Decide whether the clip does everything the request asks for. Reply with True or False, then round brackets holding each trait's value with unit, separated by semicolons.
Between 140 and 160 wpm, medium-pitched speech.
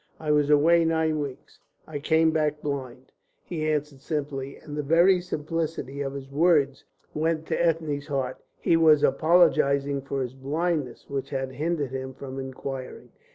True (155 wpm; 145 Hz)